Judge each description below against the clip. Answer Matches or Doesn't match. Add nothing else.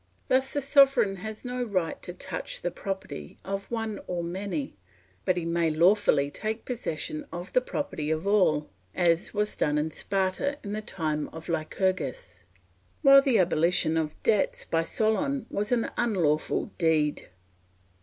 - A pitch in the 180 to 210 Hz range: Matches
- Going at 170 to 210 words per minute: Doesn't match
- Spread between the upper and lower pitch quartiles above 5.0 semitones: Matches